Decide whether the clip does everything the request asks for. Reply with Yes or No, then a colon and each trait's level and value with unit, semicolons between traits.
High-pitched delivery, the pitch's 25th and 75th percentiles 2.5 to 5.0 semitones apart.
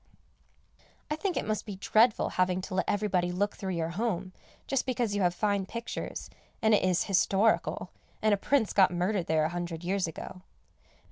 Yes: high, 195 Hz; average, 3.2 semitones